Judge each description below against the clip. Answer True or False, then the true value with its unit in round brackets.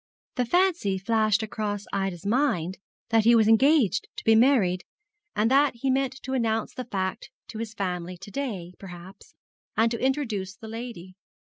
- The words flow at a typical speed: True (170 wpm)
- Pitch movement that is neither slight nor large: True (4.5 semitones)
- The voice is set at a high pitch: True (220 Hz)